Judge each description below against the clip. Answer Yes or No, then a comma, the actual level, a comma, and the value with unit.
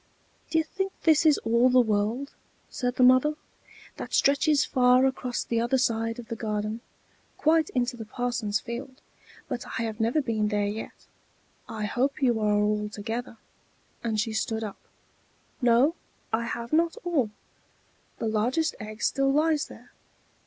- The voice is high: Yes, high, 240 Hz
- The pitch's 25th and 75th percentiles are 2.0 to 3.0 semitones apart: No, average, 3.6 semitones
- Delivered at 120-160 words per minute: Yes, average, 155 wpm